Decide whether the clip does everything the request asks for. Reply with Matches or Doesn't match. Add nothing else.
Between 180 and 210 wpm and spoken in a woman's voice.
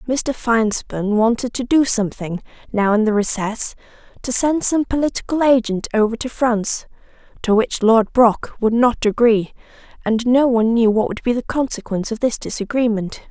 Doesn't match